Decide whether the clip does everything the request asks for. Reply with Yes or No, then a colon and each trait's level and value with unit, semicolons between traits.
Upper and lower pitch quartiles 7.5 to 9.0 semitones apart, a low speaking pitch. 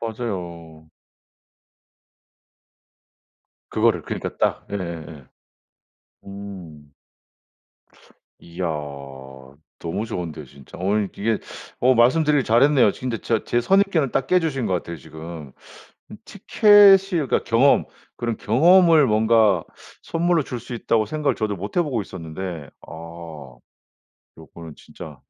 Yes: wide, 8.0 semitones; low, 105 Hz